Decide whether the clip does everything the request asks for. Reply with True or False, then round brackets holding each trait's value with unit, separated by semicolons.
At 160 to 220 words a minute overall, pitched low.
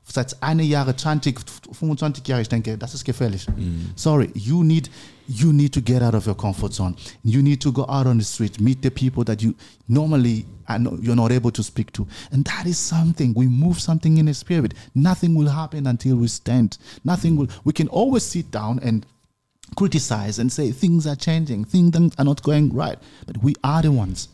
True (185 wpm; 130 Hz)